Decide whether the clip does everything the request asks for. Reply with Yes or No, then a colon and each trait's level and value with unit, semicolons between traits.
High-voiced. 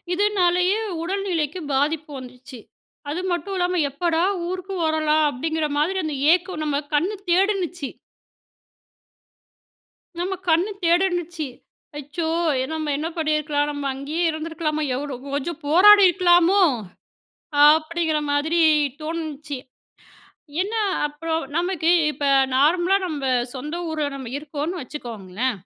Yes: very high, 320 Hz